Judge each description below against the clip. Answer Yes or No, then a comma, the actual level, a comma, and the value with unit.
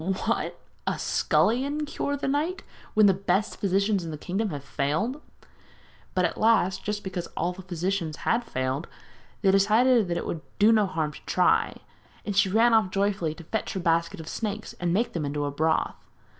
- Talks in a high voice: Yes, high, 195 Hz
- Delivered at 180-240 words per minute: Yes, average, 185 wpm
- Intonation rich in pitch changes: No, average, 4.5 semitones